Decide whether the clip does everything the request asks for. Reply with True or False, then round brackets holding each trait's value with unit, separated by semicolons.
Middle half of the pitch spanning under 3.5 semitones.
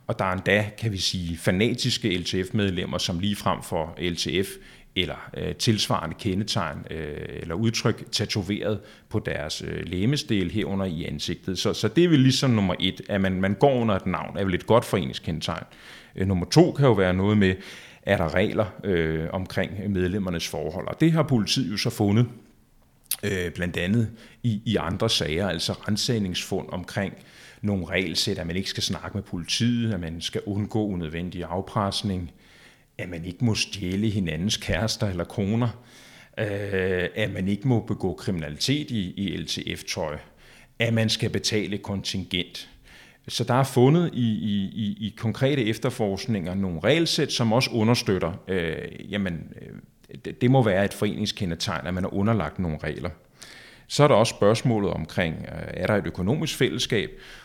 False (3.8 semitones)